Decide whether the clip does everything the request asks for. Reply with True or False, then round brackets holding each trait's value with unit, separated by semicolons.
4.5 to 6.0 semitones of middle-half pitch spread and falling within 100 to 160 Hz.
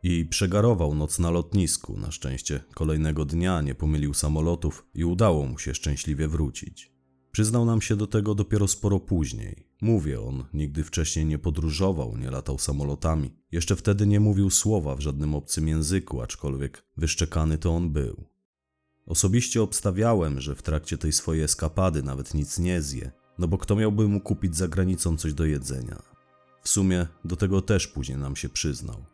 False (4.8 semitones; 80 Hz)